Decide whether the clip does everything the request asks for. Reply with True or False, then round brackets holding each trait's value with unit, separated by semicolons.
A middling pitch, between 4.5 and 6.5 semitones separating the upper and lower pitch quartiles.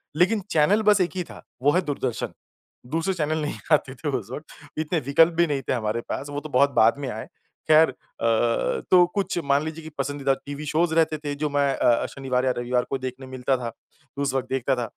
False (145 Hz; 3.6 semitones)